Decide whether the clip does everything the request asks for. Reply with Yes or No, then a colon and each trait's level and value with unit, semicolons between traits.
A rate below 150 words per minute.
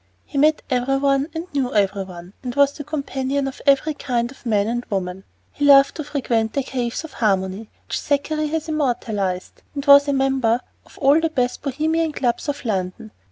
No: average, 200 wpm